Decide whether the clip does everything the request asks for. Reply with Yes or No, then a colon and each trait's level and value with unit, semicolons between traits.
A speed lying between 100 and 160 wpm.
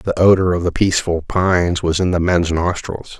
No: fast, 205 wpm